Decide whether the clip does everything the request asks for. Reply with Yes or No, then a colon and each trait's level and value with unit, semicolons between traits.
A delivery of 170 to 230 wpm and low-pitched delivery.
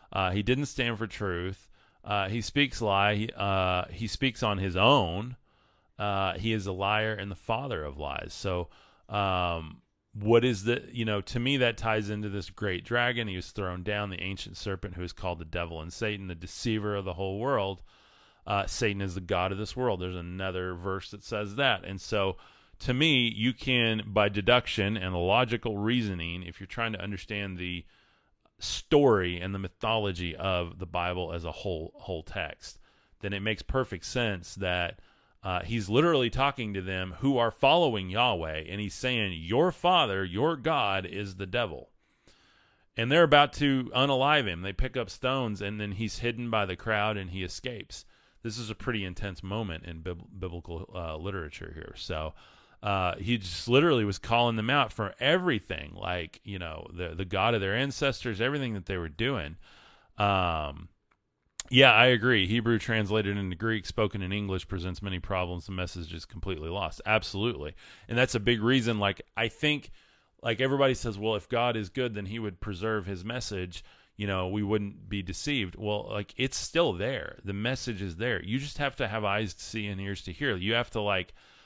Yes: average, 190 wpm; low, 105 Hz